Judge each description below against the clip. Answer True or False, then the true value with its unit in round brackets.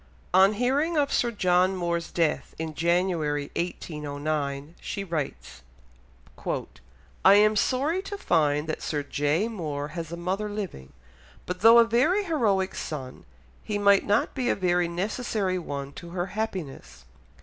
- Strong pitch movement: True (5.7 semitones)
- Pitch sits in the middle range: True (180 Hz)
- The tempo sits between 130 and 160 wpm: True (145 wpm)